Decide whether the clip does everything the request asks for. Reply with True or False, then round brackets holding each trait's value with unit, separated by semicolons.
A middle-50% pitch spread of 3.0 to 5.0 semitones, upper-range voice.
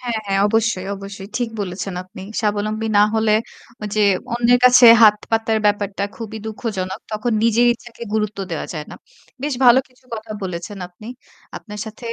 False (2.6 semitones; 215 Hz)